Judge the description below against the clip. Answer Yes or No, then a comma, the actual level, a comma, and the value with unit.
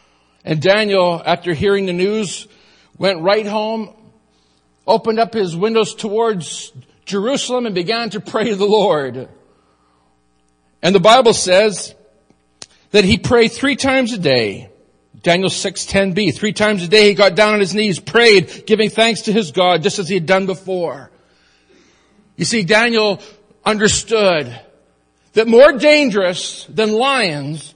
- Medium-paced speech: Yes, average, 145 wpm